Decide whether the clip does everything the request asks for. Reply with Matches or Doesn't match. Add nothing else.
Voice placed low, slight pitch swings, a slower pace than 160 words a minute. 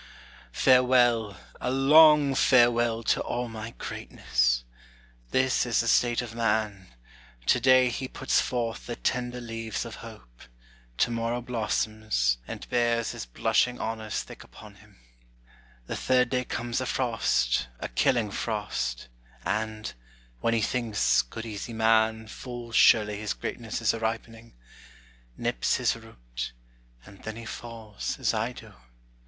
Matches